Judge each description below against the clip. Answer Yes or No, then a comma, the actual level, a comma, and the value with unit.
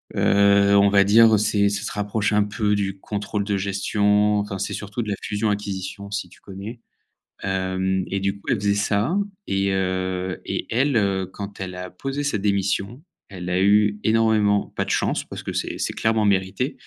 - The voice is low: Yes, low, 100 Hz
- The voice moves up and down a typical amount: No, narrow, 1.3 semitones